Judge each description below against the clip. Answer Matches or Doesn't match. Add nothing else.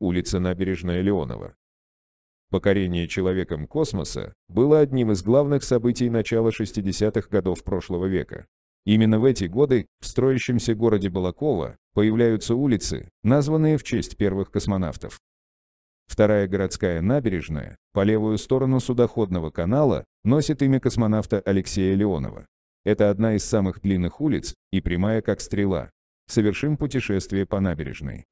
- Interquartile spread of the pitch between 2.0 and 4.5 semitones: Matches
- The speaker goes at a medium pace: Matches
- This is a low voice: Matches